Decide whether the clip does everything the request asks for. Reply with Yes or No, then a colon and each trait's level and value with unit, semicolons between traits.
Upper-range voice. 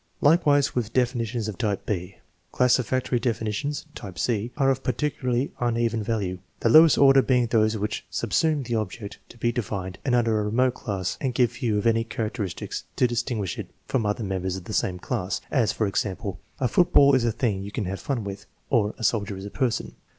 No: low, 115 Hz